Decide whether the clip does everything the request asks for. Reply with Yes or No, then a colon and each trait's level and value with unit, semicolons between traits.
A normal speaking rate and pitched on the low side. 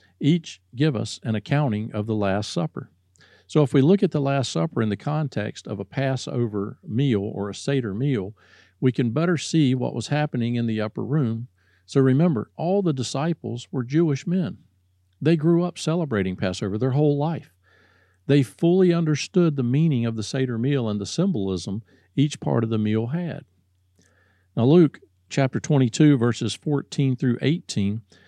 Yes: average, 175 wpm; low, 130 Hz